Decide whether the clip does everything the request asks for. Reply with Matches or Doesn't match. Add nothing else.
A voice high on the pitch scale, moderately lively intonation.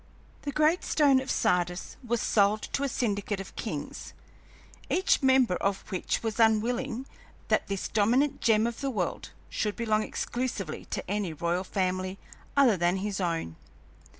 Matches